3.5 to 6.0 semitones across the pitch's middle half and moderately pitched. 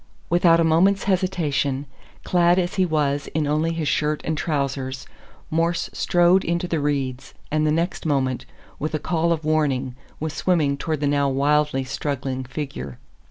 No: average, 3.1 semitones; medium, 155 Hz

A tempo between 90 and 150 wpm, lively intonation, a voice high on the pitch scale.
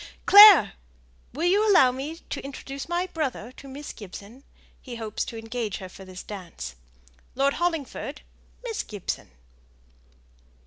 Yes: slow, 135 wpm; wide, 7.1 semitones; very high, 270 Hz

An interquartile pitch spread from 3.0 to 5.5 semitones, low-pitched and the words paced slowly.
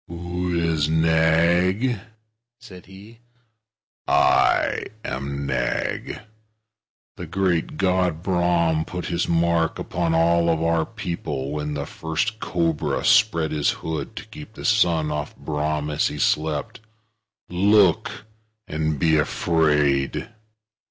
No: narrow, 2.5 semitones; very low, 80 Hz; slow, 110 wpm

